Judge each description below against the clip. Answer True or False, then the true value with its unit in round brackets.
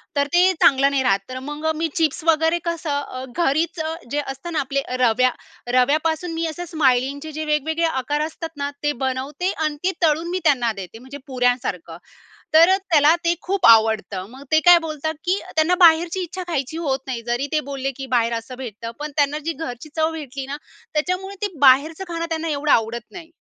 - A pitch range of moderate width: True (3.9 semitones)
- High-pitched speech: True (295 Hz)